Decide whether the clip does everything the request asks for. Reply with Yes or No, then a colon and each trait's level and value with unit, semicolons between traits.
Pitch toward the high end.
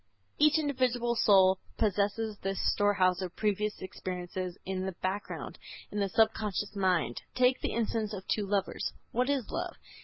Yes: high, 205 Hz